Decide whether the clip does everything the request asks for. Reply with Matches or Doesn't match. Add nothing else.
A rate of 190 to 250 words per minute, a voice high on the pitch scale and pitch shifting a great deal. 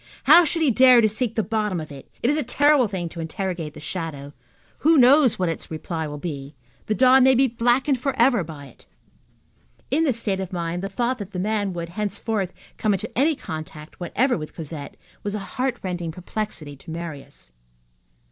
Matches